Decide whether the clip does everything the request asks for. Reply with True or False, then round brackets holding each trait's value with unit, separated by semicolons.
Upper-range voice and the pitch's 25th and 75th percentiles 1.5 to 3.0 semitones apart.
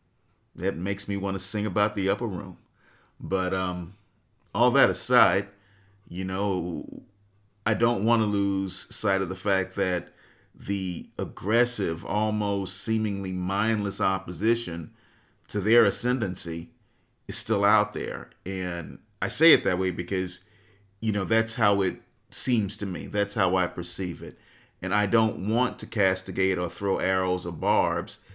False (100 Hz; 2.5 semitones)